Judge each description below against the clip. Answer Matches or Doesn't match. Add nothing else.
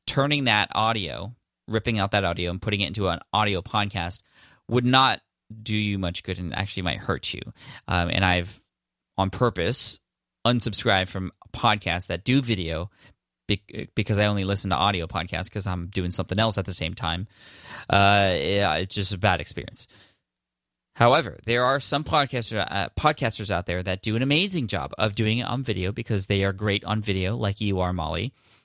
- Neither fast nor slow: Matches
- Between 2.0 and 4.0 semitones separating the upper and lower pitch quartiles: Matches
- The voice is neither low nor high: Doesn't match